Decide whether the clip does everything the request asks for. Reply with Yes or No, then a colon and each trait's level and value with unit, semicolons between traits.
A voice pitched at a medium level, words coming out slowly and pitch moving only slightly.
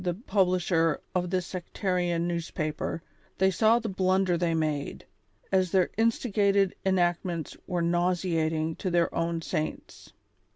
Yes: medium, 175 Hz; slow, 130 wpm; narrow, 2.2 semitones